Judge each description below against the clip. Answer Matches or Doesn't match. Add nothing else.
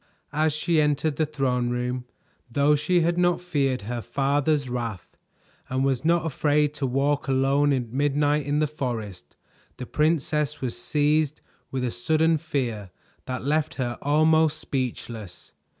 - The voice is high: Doesn't match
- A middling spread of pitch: Matches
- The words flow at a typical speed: Matches